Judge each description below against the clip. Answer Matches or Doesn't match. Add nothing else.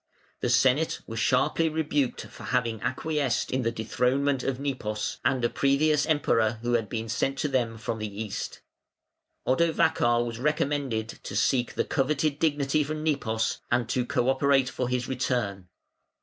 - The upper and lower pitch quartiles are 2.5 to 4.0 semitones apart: Matches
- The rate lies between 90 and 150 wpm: Doesn't match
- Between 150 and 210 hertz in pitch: Doesn't match